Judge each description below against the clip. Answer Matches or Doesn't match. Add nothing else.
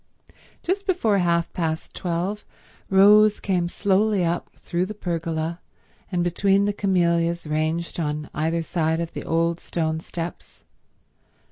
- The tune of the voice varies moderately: Matches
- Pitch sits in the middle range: Matches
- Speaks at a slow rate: Matches